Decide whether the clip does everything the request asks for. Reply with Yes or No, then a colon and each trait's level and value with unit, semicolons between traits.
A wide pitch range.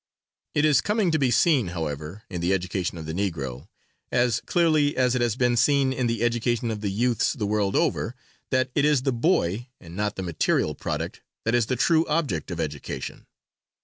Yes: wide, 6.0 semitones